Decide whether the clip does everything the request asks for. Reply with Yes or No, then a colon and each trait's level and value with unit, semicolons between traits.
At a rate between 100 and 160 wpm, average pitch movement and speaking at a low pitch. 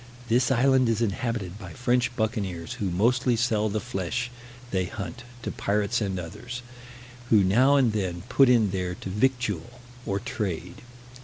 Yes: average, 155 wpm; average, 4.2 semitones; low, 110 Hz